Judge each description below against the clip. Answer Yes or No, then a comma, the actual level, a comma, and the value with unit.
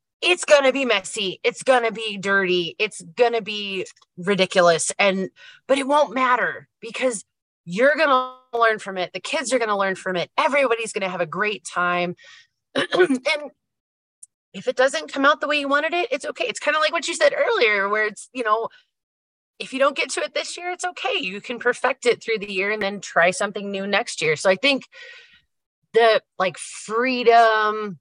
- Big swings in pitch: Yes, wide, 6.5 semitones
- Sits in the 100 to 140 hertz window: No, high, 230 Hz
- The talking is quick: Yes, fast, 210 wpm